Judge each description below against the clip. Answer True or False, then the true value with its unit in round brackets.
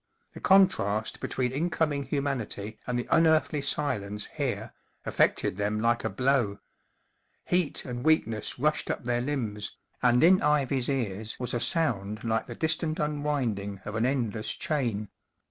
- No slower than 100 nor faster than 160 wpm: True (145 wpm)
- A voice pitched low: True (125 Hz)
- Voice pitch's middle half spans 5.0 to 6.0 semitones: True (5.5 semitones)